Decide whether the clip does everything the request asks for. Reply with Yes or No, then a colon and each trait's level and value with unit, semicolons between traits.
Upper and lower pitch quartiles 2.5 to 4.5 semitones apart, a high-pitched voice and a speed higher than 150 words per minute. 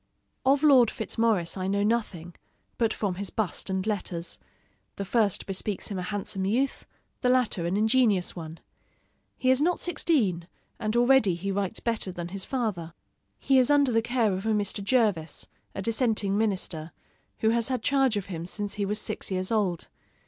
Yes: average, 4.0 semitones; high, 210 Hz; average, 180 wpm